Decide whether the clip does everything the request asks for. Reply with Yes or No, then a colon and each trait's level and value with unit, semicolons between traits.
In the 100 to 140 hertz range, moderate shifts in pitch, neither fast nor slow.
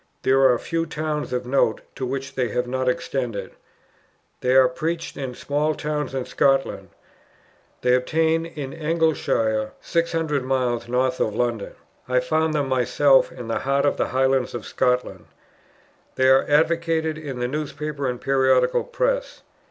Yes: low, 135 Hz; average, 3.6 semitones; average, 150 wpm